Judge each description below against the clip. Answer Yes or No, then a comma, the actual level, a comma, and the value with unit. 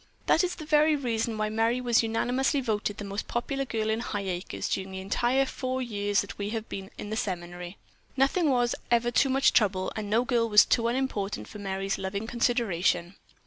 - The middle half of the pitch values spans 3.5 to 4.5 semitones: Yes, average, 3.8 semitones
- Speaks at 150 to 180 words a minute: No, average, 190 wpm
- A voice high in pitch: Yes, high, 225 Hz